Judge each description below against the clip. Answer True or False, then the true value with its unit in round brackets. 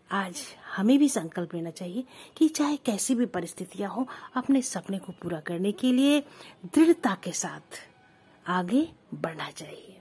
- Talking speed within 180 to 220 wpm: False (150 wpm)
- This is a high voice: True (205 Hz)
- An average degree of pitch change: False (6.7 semitones)